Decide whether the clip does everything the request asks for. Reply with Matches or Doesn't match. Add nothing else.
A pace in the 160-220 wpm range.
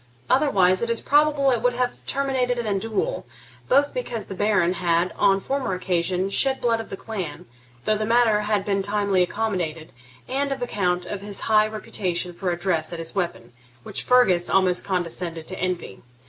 Matches